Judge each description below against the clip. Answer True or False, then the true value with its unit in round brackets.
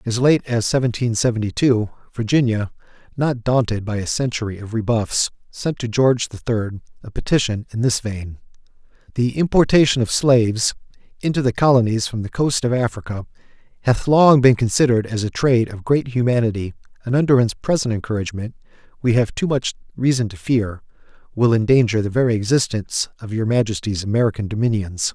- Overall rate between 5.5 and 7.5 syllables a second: True (5.8 syllables/s)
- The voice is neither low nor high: False (115 Hz)